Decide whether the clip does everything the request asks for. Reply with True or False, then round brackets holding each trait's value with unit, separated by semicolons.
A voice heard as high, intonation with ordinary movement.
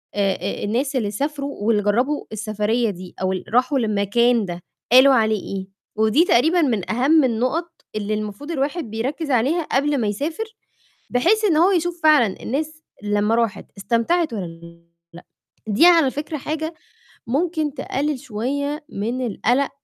False (250 Hz; 6.0 semitones)